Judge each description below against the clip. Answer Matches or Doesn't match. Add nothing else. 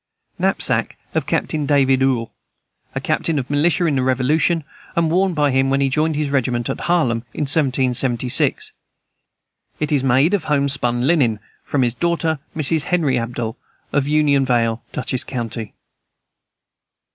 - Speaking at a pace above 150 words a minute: Doesn't match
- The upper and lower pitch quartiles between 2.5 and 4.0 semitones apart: Matches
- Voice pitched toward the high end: Doesn't match